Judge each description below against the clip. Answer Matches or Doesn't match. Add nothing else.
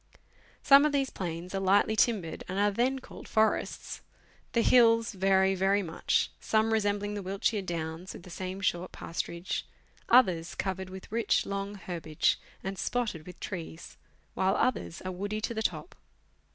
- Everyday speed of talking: Matches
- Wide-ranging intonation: Doesn't match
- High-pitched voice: Matches